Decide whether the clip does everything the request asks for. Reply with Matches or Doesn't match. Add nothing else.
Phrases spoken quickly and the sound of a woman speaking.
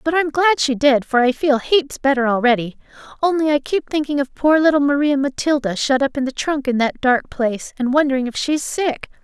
Matches